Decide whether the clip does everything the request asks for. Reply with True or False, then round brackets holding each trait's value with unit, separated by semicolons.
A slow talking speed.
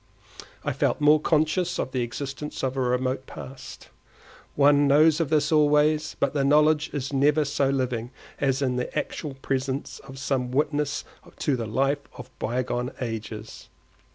False (155 wpm)